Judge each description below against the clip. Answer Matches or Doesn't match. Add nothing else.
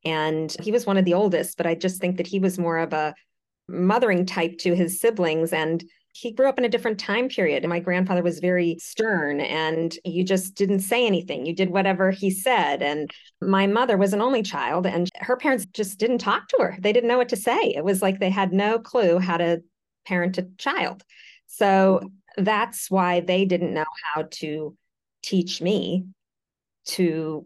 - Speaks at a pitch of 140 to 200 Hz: Matches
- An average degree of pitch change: Matches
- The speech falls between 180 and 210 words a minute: Matches